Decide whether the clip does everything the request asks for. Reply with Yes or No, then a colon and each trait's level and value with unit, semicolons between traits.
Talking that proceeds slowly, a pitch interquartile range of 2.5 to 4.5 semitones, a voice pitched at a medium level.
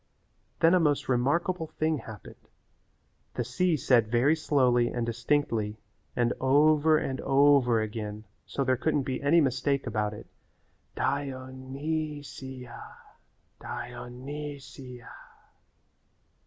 No: slow, 130 wpm; average, 3.4 semitones; low, 130 Hz